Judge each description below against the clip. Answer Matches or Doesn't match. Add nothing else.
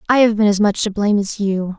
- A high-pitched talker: Matches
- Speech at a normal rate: Doesn't match